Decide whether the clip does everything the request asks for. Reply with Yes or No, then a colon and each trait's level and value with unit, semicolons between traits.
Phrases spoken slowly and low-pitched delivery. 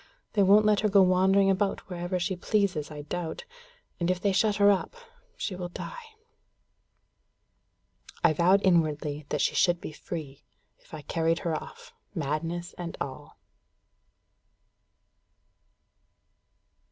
No: slow, 130 wpm; medium, 180 Hz